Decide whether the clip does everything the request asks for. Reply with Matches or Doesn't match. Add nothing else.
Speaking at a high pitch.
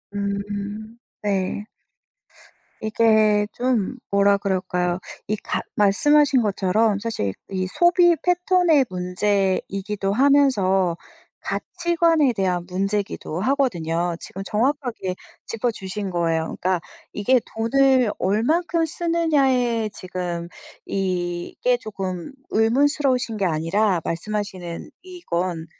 Matches